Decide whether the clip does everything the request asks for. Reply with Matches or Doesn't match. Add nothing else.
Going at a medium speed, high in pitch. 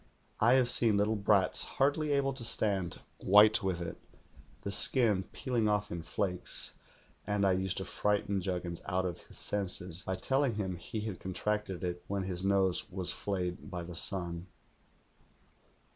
Doesn't match